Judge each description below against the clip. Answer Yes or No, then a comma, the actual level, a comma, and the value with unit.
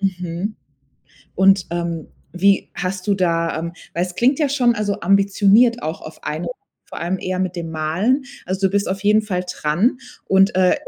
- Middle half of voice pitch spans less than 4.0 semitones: Yes, average, 2.9 semitones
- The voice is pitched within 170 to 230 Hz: Yes, high, 190 Hz